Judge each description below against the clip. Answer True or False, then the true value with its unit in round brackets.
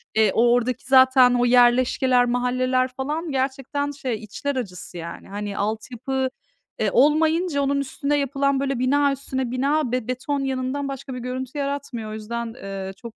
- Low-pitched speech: False (255 Hz)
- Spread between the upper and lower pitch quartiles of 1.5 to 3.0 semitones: True (2.6 semitones)